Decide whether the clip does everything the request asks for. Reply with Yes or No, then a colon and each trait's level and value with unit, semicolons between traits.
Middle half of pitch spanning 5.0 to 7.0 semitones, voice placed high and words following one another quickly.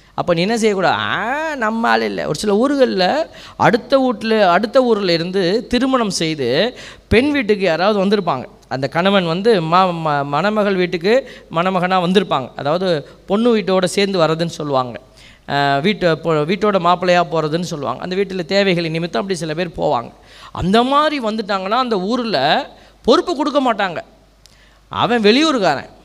Yes: average, 5.3 semitones; high, 195 Hz; fast, 140 wpm